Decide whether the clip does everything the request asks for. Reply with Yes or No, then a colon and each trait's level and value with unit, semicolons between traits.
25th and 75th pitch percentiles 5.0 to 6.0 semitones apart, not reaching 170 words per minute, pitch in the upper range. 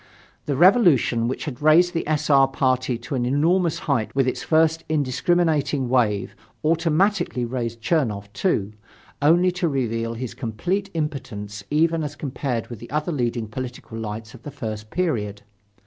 No: wide, 5.5 semitones; average, 155 wpm; low, 135 Hz